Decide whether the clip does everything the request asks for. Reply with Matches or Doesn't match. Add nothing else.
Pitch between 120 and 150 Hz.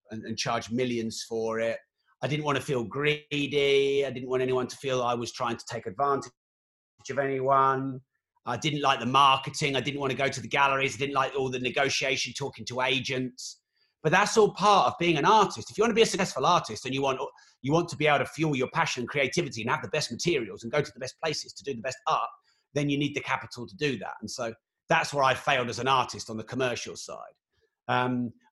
Matches